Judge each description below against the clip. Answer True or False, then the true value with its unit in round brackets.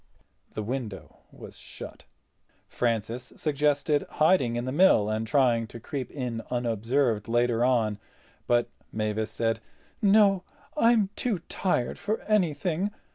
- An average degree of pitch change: False (5.7 semitones)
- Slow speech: True (125 wpm)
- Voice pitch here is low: True (125 Hz)